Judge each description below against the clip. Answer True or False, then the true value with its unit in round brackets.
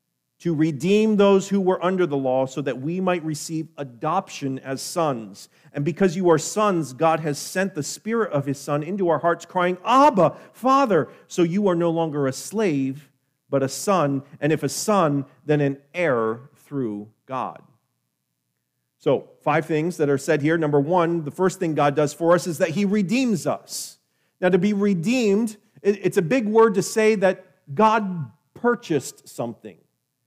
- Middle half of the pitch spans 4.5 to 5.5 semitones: True (5.2 semitones)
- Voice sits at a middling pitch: True (165 Hz)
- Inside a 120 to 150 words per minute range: False (175 wpm)